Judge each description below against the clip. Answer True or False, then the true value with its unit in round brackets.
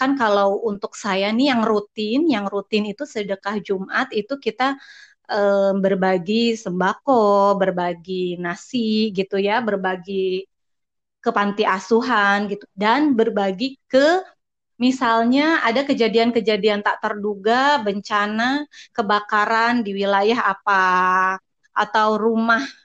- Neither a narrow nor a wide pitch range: True (3.0 semitones)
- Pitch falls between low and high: False (215 Hz)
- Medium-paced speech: True (110 wpm)